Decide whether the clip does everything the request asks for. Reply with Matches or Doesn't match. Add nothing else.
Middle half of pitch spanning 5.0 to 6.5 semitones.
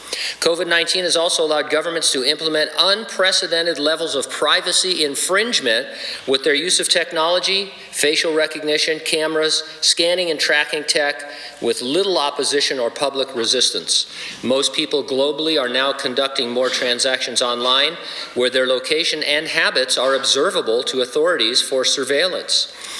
Doesn't match